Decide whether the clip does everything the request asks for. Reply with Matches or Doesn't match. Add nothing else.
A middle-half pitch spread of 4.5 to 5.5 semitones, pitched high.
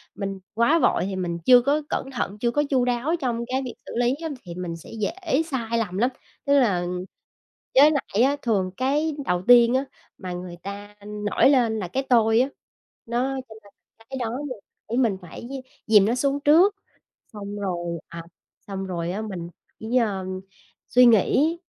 Matches